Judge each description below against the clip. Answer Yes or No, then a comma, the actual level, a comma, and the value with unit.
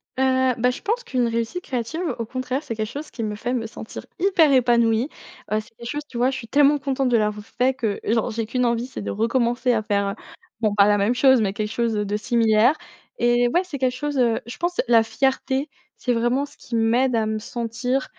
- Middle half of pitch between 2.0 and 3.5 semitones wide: Yes, average, 2.8 semitones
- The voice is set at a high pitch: Yes, high, 240 Hz